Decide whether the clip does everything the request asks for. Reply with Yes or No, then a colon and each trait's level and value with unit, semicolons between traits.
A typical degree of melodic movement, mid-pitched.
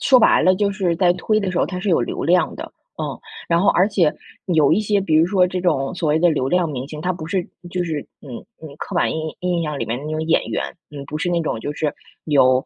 Yes: average, 3.3 semitones; medium, 170 Hz